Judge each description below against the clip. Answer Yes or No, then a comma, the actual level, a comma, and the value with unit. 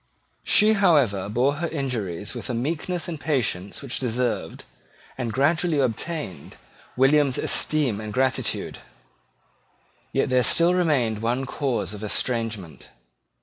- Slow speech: Yes, slow, 120 wpm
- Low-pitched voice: Yes, low, 130 Hz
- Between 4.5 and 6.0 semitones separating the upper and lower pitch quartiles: Yes, average, 5.2 semitones